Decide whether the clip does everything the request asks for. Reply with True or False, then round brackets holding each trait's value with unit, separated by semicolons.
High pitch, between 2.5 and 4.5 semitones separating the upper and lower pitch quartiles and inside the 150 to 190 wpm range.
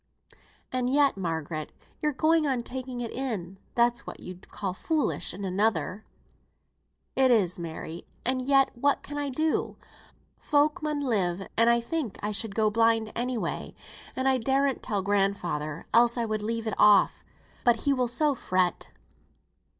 False (230 Hz; 5.1 semitones; 160 wpm)